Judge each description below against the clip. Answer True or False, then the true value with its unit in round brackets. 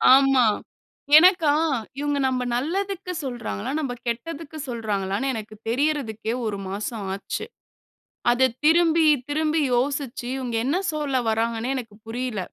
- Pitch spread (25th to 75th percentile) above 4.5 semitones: True (5.1 semitones)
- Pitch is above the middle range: True (260 Hz)